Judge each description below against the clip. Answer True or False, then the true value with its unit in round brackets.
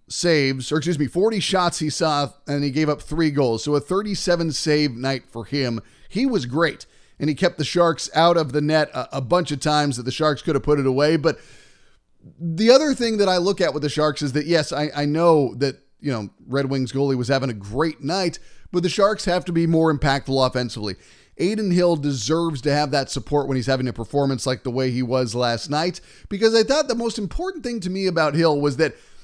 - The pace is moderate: False (235 wpm)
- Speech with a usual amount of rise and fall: True (4.4 semitones)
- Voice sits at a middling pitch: True (150 Hz)